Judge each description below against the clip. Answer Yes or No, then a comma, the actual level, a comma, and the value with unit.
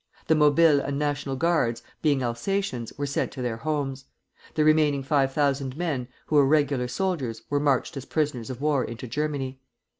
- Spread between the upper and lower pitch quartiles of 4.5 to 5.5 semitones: No, narrow, 2.6 semitones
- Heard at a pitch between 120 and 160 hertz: Yes, medium, 140 Hz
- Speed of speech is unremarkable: Yes, average, 175 wpm